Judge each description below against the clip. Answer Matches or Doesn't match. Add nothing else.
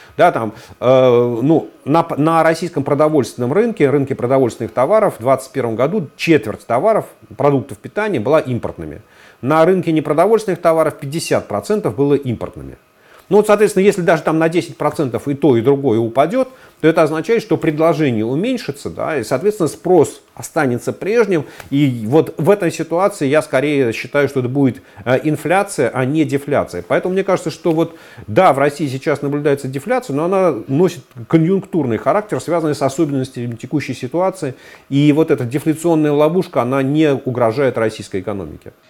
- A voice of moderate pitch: Matches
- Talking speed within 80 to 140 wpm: Doesn't match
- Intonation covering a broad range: Doesn't match